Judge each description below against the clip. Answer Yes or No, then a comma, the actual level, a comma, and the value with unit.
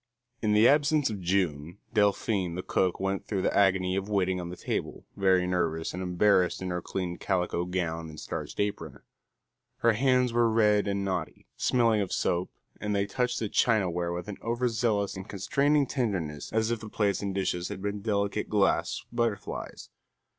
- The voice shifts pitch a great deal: No, average, 3.3 semitones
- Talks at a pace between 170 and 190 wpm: Yes, average, 180 wpm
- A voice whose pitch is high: No, low, 100 Hz